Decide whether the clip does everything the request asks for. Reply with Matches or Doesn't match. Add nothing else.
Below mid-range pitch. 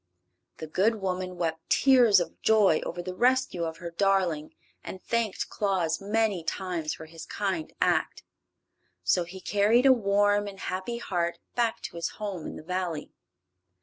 Doesn't match